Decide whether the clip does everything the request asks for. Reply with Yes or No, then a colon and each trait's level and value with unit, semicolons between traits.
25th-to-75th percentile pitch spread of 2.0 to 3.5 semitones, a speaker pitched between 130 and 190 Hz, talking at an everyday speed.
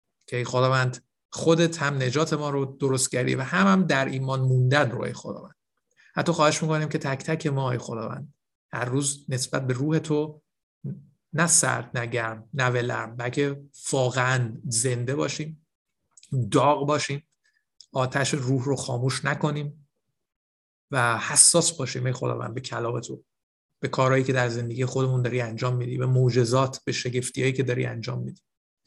No: average, 2.9 semitones; low, 135 Hz; fast, 160 wpm